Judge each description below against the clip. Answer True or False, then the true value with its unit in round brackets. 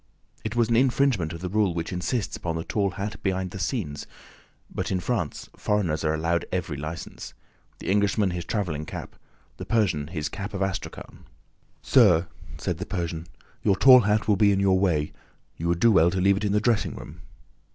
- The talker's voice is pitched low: True (95 Hz)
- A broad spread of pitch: False (3.7 semitones)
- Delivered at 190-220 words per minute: True (195 wpm)